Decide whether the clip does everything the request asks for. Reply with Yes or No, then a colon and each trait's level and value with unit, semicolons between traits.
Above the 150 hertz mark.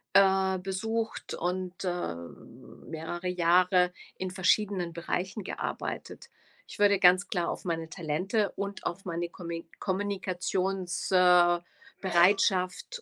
Yes: medium, 185 Hz